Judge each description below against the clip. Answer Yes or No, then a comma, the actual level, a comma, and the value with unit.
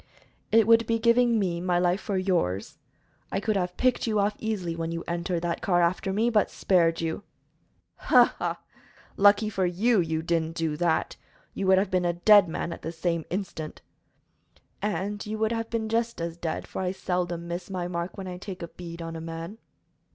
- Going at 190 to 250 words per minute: Yes, average, 200 wpm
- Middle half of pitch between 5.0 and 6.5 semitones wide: No, average, 3.6 semitones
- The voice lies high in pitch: No, medium, 180 Hz